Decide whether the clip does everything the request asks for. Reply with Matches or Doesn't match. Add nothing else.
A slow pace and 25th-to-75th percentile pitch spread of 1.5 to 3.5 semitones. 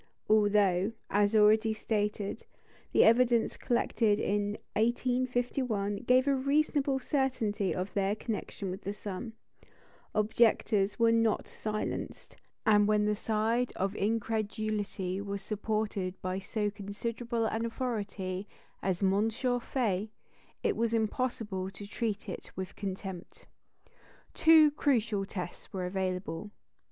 Matches